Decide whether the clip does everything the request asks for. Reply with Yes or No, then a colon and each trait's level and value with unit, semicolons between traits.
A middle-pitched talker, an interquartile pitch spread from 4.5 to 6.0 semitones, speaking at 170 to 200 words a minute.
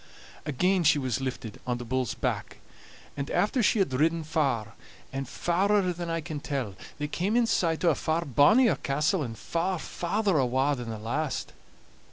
Yes: medium, 150 Hz; average, 5.2 semitones; average, 180 wpm